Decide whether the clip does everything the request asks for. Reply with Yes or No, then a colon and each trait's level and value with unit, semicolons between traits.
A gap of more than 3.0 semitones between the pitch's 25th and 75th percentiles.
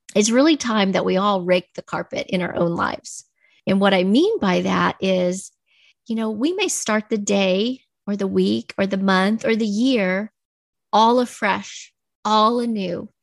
Yes: average, 3.7 semitones